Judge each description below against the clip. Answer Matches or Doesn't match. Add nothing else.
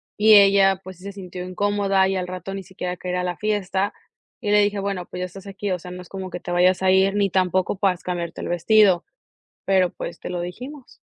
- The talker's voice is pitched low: Doesn't match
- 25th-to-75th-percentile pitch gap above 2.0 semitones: Doesn't match